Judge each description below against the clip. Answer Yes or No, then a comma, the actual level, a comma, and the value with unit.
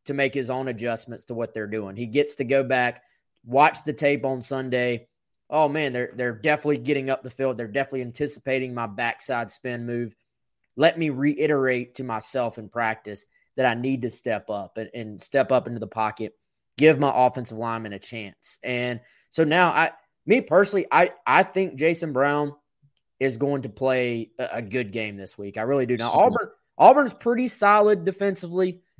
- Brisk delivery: No, average, 190 wpm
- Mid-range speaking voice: No, low, 130 Hz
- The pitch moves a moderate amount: Yes, average, 3.9 semitones